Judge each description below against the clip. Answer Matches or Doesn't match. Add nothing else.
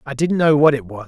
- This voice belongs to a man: Matches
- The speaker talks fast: Matches